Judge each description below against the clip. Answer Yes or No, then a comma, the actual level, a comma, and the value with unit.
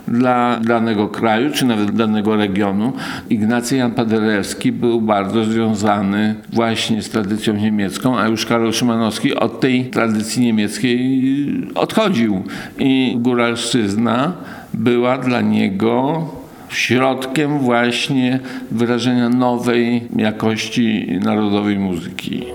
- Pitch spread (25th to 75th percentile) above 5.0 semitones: No, narrow, 2.5 semitones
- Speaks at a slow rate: Yes, slow, 100 wpm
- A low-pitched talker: Yes, low, 115 Hz